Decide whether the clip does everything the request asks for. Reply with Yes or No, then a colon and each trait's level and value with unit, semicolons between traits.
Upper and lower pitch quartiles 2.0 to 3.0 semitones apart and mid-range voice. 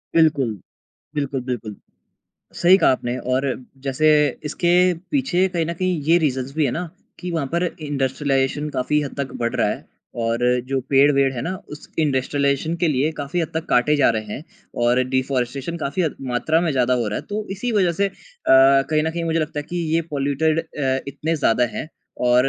No: average, 3.8 semitones; medium, 145 Hz